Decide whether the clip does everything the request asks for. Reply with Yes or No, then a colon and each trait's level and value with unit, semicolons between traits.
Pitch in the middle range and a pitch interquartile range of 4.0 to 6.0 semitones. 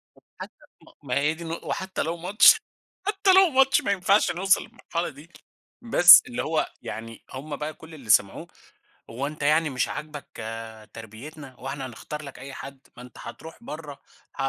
Yes: medium, 155 Hz; average, 4.7 semitones